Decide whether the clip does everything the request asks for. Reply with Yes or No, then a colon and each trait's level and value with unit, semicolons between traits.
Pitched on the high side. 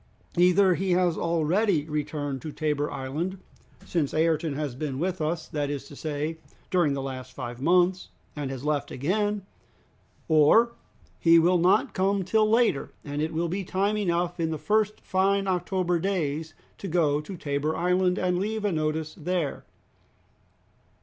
No: medium, 165 Hz